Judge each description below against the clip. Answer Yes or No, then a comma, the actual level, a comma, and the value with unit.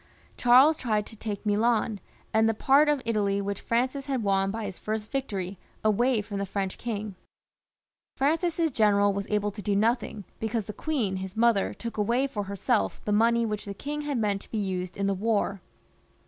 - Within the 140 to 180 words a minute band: No, average, 190 wpm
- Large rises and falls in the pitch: No, average, 3.1 semitones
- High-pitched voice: Yes, high, 215 Hz